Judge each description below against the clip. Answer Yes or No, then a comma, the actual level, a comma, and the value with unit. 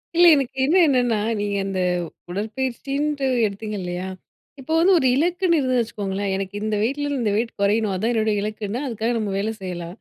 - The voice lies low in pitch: No, high, 220 Hz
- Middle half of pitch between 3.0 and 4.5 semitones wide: No, average, 5.0 semitones